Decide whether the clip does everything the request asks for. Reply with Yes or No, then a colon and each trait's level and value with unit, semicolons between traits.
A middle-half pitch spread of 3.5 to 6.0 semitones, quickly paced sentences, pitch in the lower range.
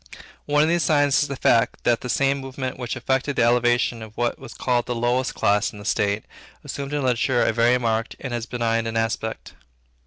No: average, 2.7 semitones; fast, 215 wpm; low, 120 Hz